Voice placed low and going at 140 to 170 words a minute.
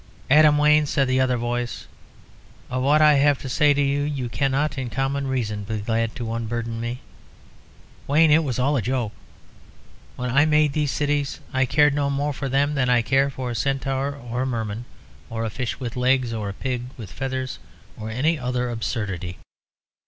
No: low, 130 Hz; average, 185 wpm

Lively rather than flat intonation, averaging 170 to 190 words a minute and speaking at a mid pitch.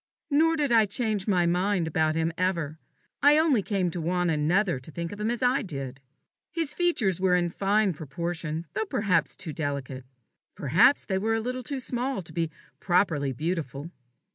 Yes: wide, 5.7 semitones; average, 180 wpm; medium, 180 Hz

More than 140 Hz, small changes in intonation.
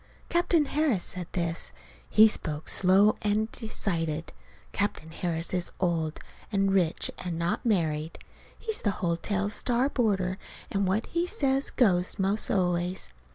No: high, 190 Hz; average, 4.1 semitones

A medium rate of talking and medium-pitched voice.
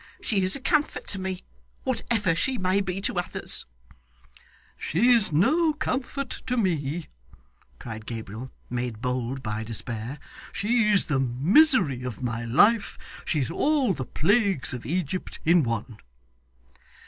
No: slow, 130 wpm; medium, 175 Hz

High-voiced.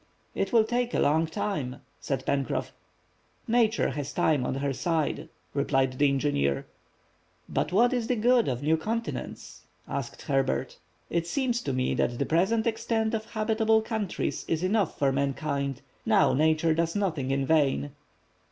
No: medium, 160 Hz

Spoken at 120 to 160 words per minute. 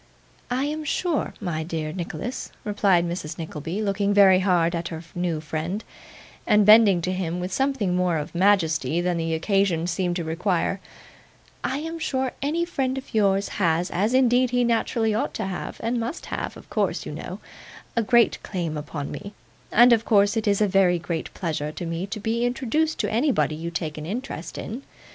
No: average, 190 wpm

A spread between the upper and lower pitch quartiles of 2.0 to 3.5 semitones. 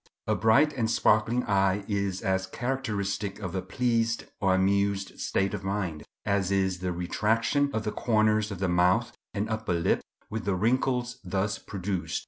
Yes: average, 2.8 semitones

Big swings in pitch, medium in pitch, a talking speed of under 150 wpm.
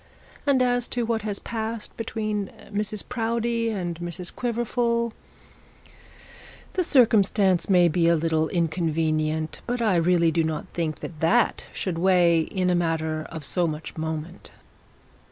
Yes: wide, 5.7 semitones; medium, 180 Hz; average, 140 wpm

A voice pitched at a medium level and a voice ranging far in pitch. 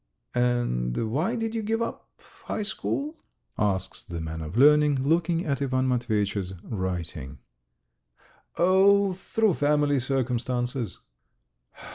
No: low, 130 Hz; wide, 9.0 semitones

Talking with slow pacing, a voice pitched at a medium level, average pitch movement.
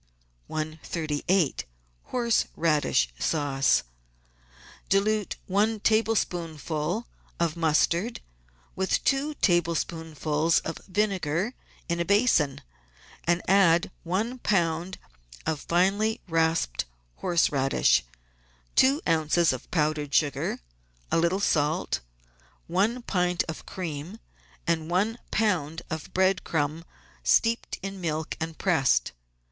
Yes: slow, 100 wpm; medium, 170 Hz; average, 4.0 semitones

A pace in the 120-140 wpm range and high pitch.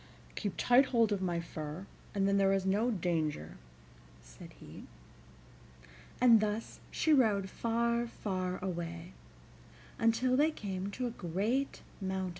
Yes: slow, 135 wpm; high, 200 Hz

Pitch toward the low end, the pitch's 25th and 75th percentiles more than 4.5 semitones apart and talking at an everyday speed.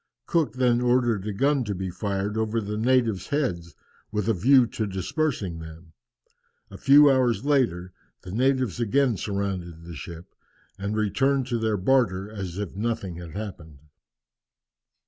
Yes: low, 105 Hz; average, 5.3 semitones; average, 150 wpm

